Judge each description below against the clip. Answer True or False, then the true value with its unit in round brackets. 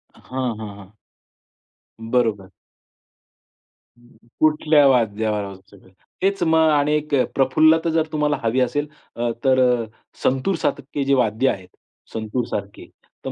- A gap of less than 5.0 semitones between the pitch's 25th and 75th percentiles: False (5.3 semitones)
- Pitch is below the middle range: True (130 Hz)